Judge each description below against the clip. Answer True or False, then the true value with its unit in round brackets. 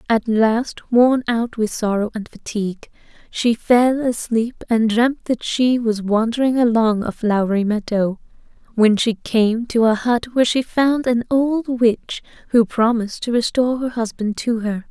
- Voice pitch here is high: True (230 Hz)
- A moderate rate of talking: True (165 wpm)